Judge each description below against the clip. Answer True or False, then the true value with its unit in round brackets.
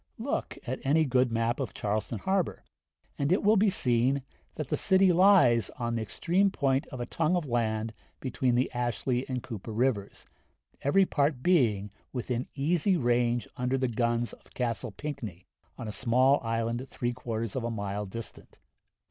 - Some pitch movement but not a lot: True (3.5 semitones)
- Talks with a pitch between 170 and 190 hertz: False (125 Hz)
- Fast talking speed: False (170 wpm)